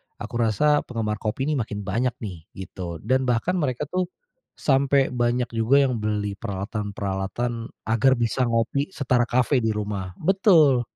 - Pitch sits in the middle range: No, low, 120 Hz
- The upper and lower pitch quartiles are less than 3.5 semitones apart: No, average, 4.1 semitones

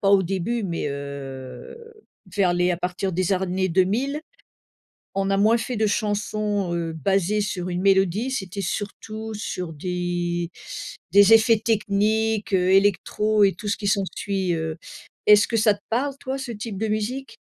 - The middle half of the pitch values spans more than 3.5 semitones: No, average, 3.2 semitones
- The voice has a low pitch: No, high, 200 Hz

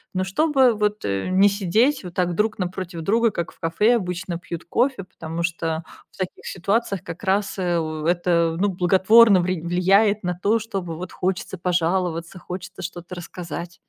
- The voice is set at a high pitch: No, medium, 180 Hz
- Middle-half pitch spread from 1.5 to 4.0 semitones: Yes, average, 2.9 semitones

